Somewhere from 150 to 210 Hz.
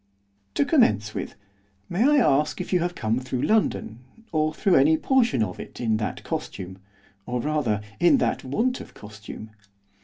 No: medium, 140 Hz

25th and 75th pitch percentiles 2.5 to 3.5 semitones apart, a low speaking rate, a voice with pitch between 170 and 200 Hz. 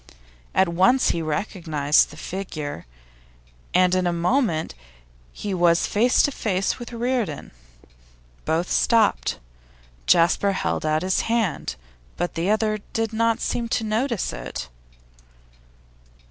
No: average, 5.1 semitones; slow, 120 wpm; high, 190 Hz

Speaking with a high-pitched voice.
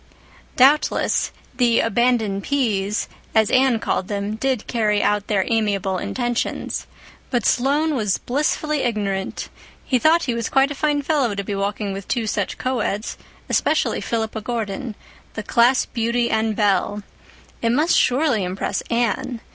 Yes: high, 230 Hz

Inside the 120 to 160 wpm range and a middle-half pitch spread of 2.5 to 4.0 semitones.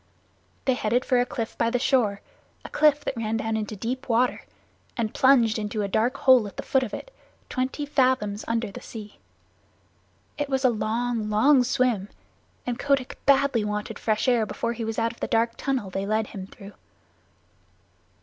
No: average, 185 wpm; average, 3.2 semitones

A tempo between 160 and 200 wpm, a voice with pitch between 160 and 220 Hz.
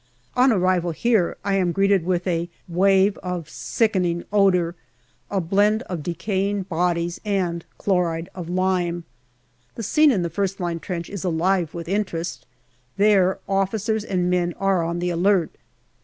No: average, 150 wpm; medium, 185 Hz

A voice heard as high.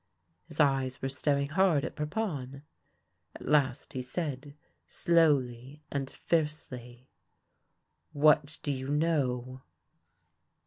No: medium, 140 Hz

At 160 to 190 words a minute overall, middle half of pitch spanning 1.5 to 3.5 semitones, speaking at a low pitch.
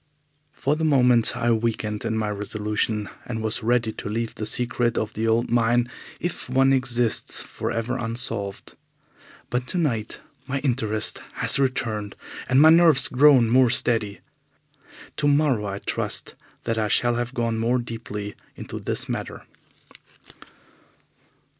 No: average, 140 wpm; narrow, 2.6 semitones; low, 120 Hz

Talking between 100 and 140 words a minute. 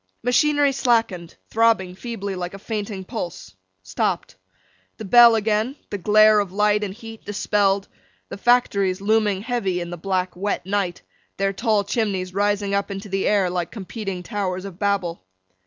No: average, 155 wpm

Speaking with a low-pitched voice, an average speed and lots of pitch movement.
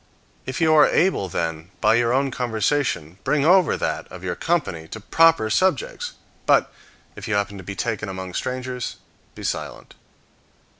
Yes: low, 120 Hz; average, 160 wpm; wide, 8.0 semitones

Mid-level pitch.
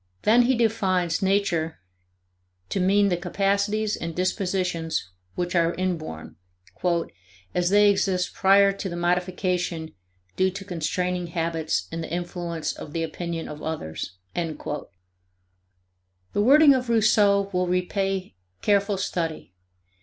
Yes: medium, 180 Hz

